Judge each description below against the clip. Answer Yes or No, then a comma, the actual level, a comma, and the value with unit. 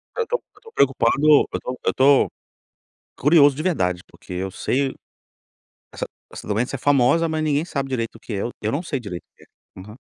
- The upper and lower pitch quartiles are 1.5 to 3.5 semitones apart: No, average, 5.0 semitones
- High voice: No, low, 135 Hz